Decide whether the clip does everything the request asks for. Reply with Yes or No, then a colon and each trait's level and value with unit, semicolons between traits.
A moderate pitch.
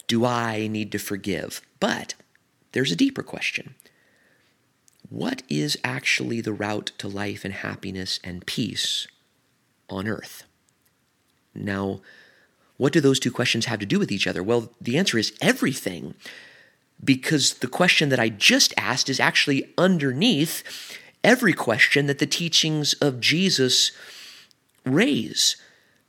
No: low, 120 Hz